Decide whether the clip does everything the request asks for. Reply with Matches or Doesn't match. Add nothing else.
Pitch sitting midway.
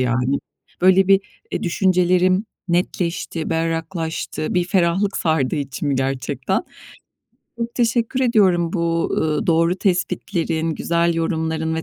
Matches